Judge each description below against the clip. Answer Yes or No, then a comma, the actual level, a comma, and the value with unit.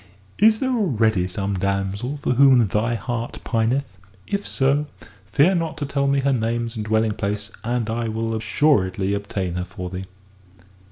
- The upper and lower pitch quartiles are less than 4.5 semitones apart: No, wide, 5.4 semitones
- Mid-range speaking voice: No, low, 115 Hz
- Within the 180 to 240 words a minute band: No, average, 165 wpm